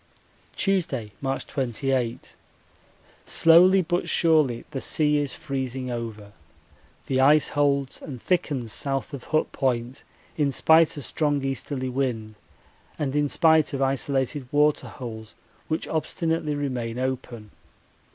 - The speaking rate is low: Yes, slow, 120 wpm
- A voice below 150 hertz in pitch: Yes, low, 135 Hz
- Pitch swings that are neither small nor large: Yes, average, 3.1 semitones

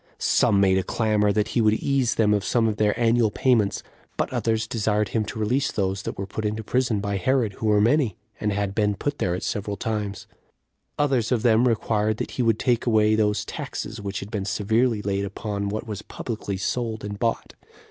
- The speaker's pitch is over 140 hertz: No, low, 110 Hz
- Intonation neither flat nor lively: No, narrow, 2.1 semitones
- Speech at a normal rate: No, fast, 210 wpm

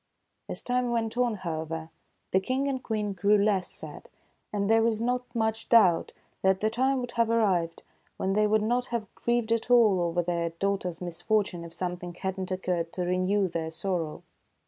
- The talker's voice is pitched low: No, high, 200 Hz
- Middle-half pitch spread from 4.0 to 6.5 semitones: Yes, average, 4.4 semitones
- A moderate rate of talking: Yes, average, 190 wpm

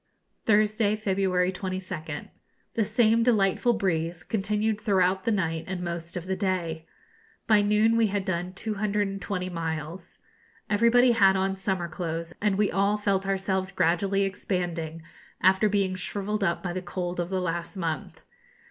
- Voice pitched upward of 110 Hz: Yes, high, 190 Hz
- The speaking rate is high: No, average, 150 wpm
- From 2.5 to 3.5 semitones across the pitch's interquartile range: Yes, average, 2.8 semitones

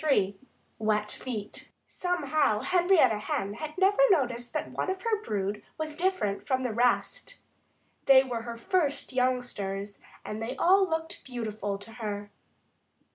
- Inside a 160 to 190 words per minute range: No, slow, 135 wpm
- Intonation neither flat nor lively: No, wide, 7.5 semitones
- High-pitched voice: Yes, high, 245 Hz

